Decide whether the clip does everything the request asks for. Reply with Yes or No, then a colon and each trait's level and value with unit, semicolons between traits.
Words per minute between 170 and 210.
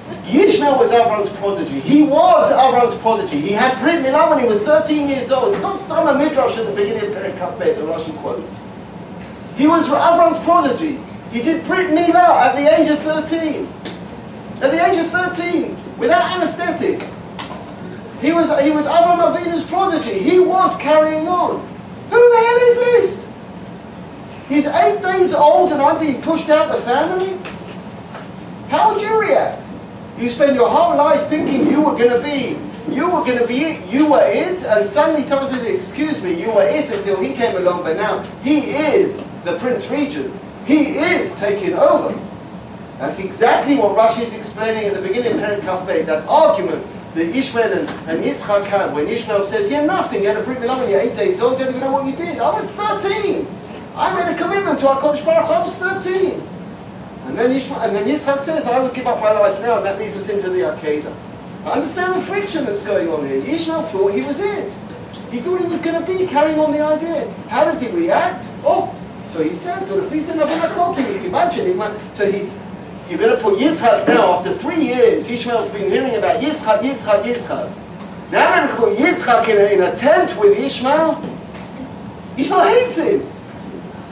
Yes: average, 190 wpm